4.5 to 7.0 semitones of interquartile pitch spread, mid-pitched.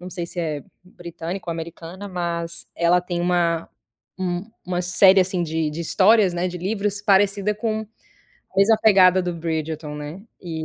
No: narrow, 2.4 semitones; medium, 180 Hz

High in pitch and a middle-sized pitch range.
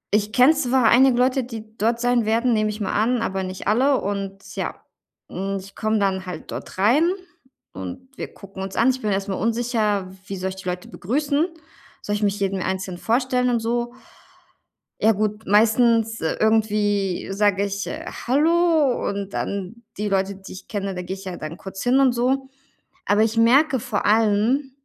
Yes: high, 215 Hz; average, 3.8 semitones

